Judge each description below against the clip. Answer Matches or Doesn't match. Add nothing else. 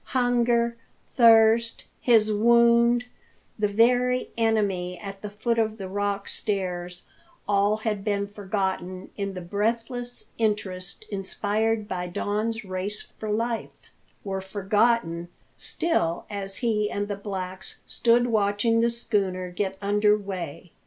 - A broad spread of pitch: Doesn't match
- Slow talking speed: Matches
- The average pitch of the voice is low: Doesn't match